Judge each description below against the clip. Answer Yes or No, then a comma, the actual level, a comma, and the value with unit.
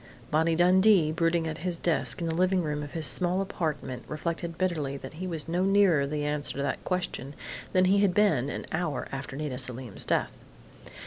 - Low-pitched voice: No, medium, 160 Hz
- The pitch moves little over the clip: No, average, 3.8 semitones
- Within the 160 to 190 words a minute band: No, average, 200 wpm